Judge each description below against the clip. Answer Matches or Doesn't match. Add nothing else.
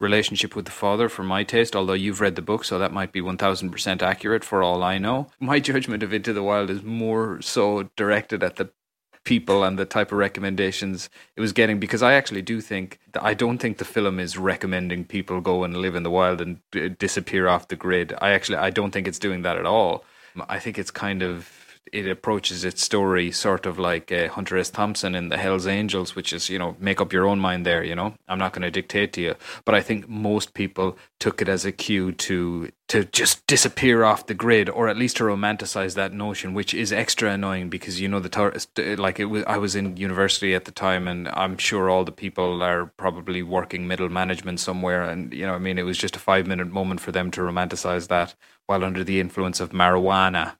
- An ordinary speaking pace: Doesn't match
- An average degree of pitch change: Doesn't match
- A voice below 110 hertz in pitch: Matches